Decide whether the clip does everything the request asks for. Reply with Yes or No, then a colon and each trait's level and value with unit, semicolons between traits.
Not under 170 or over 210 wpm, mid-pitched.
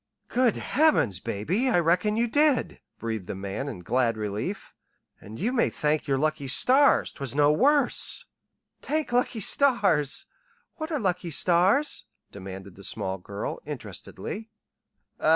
No: slow, 135 wpm; medium, 165 Hz